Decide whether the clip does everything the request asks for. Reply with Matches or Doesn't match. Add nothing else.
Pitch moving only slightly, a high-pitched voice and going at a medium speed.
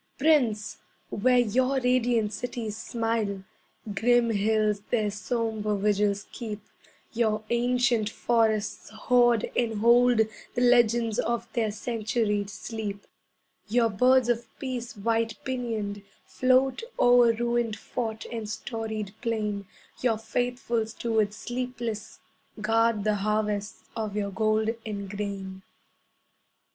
Doesn't match